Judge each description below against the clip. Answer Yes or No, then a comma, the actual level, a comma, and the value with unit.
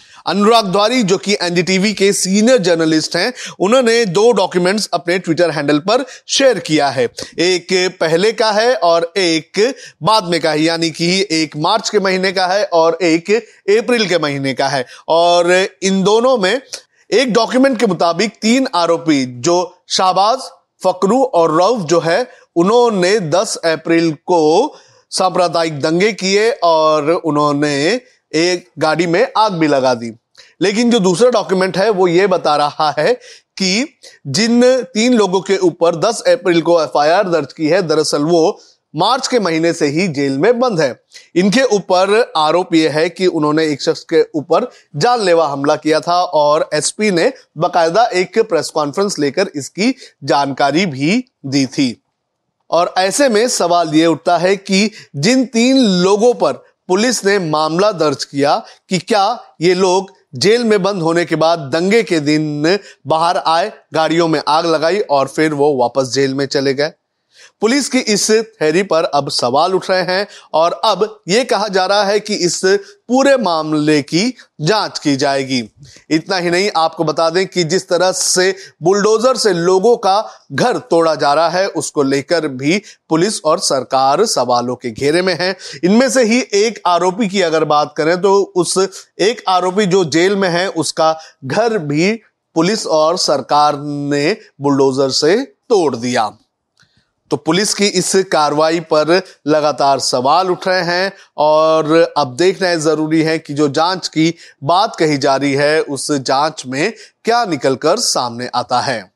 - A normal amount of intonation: Yes, average, 4.7 semitones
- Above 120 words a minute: Yes, average, 165 wpm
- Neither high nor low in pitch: Yes, medium, 175 Hz